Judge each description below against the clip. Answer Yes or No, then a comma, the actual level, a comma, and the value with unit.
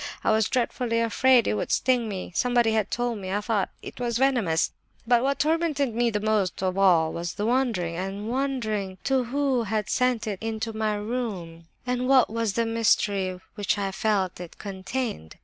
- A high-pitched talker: Yes, high, 220 Hz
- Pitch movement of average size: Yes, average, 4.2 semitones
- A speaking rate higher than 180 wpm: Yes, average, 190 wpm